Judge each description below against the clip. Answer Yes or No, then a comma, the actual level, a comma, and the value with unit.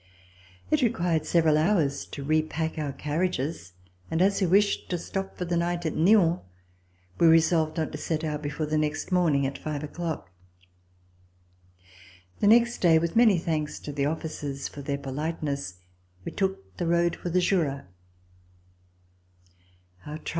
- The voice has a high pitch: No, medium, 160 Hz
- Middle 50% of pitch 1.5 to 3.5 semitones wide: Yes, average, 2.9 semitones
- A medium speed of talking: Yes, average, 155 wpm